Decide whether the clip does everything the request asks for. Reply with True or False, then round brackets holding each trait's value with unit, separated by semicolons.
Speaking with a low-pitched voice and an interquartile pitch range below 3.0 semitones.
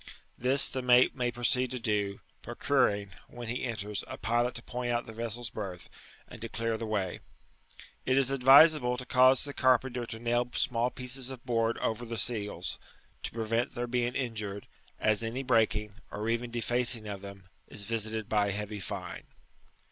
True (115 Hz; 2.5 semitones)